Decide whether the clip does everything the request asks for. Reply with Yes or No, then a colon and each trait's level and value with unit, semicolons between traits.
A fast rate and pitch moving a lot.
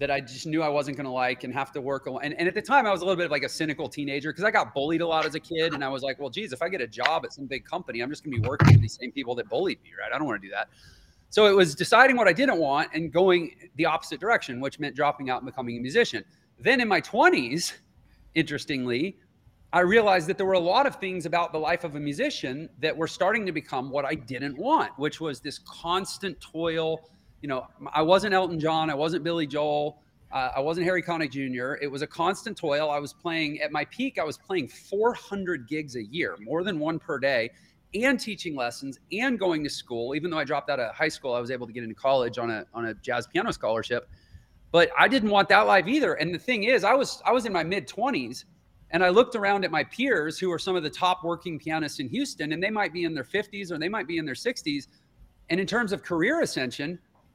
No: fast, 260 wpm; average, 5.0 semitones